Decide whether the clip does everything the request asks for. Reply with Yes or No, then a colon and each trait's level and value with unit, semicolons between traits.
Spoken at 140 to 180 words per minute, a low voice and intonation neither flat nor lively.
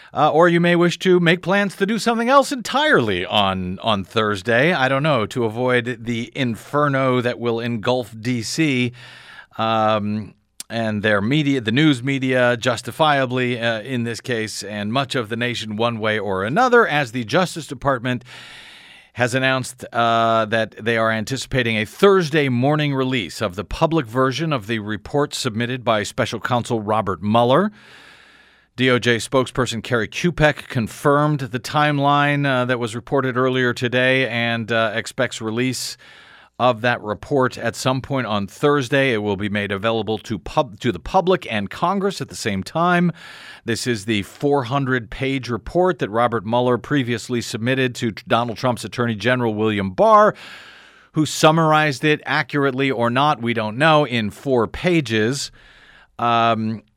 Yes: average, 155 wpm; low, 125 Hz; average, 4.1 semitones